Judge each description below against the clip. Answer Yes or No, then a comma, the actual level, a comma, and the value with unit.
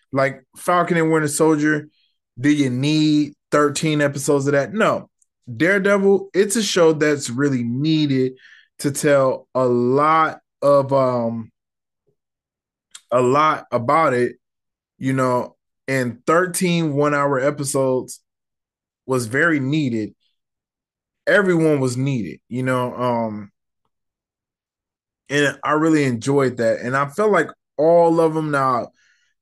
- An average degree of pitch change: Yes, average, 3.5 semitones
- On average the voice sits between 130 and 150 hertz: Yes, medium, 140 Hz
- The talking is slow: Yes, slow, 120 wpm